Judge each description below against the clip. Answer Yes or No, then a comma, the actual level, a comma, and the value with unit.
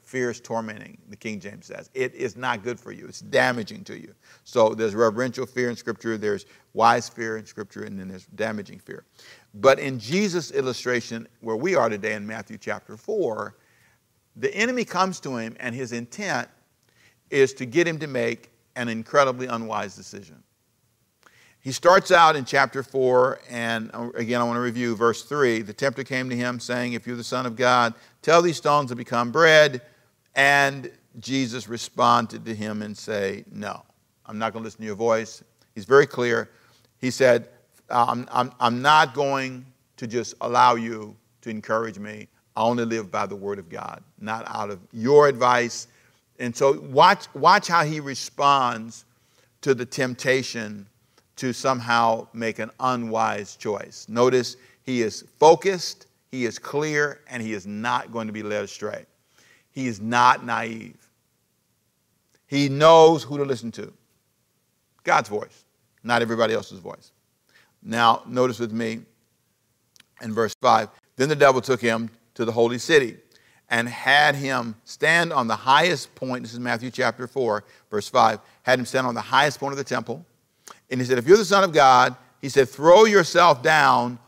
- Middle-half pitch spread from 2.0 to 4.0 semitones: Yes, average, 2.8 semitones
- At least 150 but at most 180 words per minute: Yes, average, 175 wpm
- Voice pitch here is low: Yes, low, 120 Hz